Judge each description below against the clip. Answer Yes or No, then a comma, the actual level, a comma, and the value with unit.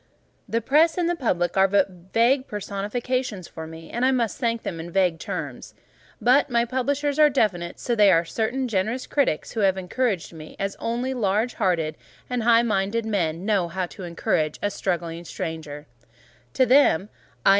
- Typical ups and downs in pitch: No, wide, 5.9 semitones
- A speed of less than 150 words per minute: No, average, 175 wpm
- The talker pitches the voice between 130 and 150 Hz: No, high, 205 Hz